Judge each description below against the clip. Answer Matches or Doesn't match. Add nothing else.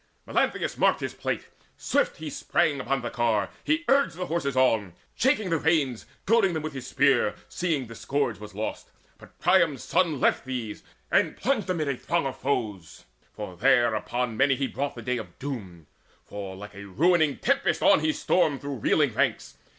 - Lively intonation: Matches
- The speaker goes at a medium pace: Matches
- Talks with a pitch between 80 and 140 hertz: Matches